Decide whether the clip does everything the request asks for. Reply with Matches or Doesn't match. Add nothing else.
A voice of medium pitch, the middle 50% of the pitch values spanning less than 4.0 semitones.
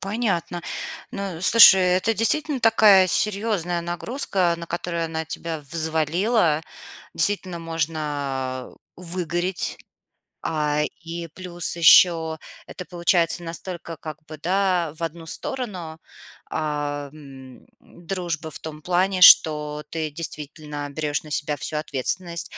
Matches